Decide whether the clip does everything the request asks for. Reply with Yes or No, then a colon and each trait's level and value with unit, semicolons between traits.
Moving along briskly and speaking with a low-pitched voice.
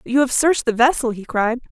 No: fast, 270 wpm; high, 245 Hz